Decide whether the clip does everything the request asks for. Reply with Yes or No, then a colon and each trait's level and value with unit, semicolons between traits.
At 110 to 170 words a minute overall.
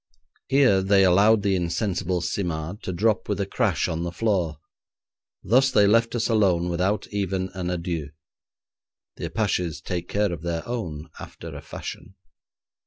Yes: average, 155 wpm